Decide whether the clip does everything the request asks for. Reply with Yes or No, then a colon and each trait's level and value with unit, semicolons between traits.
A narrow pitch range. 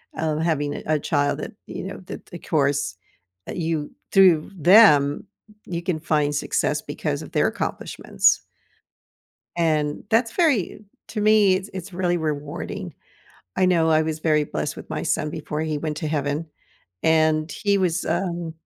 No: average, 3.3 semitones